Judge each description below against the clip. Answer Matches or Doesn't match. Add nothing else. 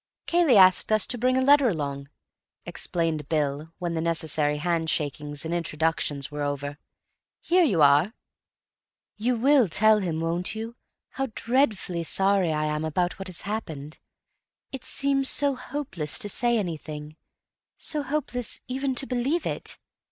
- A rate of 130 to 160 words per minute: Matches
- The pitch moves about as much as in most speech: Doesn't match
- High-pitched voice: Doesn't match